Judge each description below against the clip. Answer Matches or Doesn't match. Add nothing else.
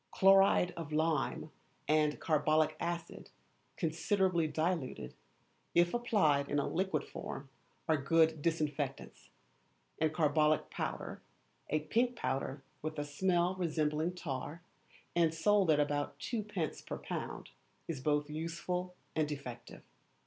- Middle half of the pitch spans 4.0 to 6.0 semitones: Doesn't match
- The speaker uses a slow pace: Matches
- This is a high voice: Doesn't match